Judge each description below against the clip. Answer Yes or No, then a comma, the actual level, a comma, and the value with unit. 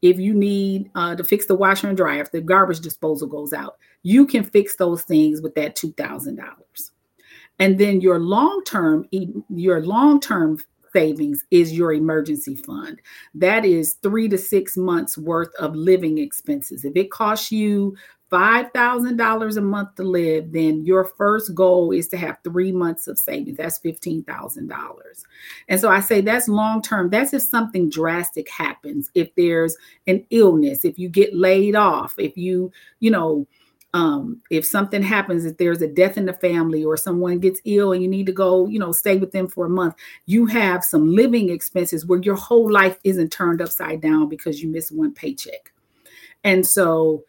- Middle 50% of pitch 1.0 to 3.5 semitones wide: No, average, 4.0 semitones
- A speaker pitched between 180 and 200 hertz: Yes, medium, 185 Hz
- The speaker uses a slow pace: No, average, 180 wpm